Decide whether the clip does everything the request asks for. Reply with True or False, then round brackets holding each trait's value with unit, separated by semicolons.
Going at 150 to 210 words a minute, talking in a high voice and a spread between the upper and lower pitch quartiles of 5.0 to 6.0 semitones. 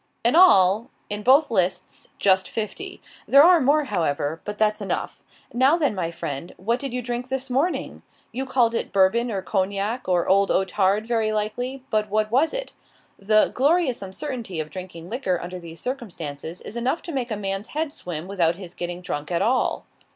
True (185 wpm; 215 Hz; 5.6 semitones)